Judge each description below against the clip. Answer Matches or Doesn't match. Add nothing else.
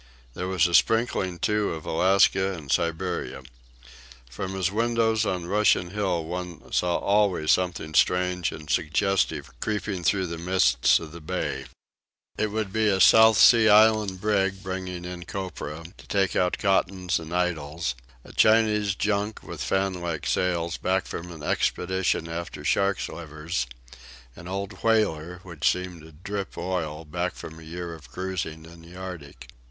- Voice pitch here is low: Matches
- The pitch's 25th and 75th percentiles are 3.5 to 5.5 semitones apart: Doesn't match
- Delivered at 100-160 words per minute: Matches